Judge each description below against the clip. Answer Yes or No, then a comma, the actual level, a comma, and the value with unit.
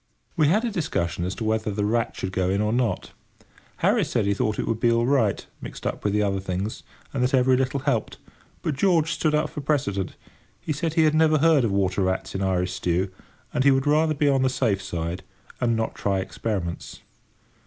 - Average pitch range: No, wide, 6.7 semitones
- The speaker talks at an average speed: No, fast, 225 wpm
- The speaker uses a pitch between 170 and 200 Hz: No, low, 115 Hz